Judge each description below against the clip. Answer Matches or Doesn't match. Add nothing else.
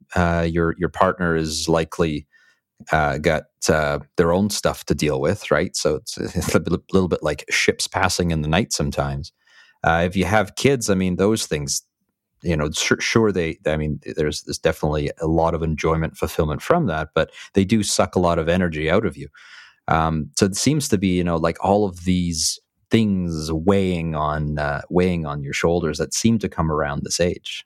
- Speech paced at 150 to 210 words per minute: Matches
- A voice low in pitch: Matches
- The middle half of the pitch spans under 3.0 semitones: Doesn't match